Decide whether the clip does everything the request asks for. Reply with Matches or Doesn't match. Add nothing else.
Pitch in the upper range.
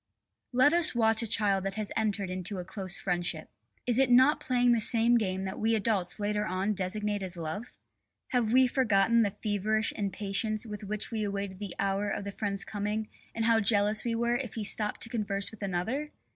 Matches